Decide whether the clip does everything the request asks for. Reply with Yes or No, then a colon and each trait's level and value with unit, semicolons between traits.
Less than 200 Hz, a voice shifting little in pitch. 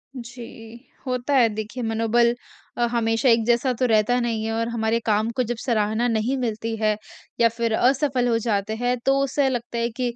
No: high, 235 Hz; narrow, 1.8 semitones